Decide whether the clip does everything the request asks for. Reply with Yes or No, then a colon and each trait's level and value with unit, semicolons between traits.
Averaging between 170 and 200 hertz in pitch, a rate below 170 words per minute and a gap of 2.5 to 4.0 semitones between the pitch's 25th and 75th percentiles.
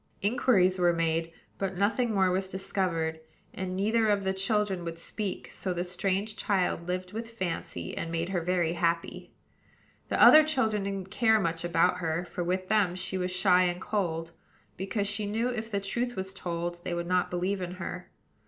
No: medium, 185 Hz; average, 185 wpm; average, 2.8 semitones